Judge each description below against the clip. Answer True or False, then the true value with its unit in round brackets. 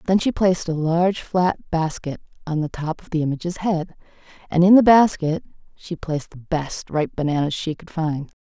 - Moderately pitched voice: True (165 Hz)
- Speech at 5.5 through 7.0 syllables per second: False (5.0 syllables/s)